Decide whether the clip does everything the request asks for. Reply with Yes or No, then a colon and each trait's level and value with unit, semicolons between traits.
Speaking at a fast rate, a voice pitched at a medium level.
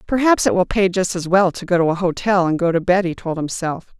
Yes: fast, 285 wpm; medium, 180 Hz